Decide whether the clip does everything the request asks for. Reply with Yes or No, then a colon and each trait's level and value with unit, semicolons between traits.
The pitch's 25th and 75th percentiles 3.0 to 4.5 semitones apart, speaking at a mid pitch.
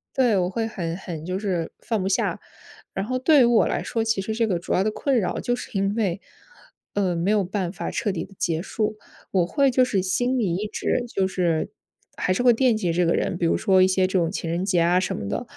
No: average, 4.0 semitones; high, 195 Hz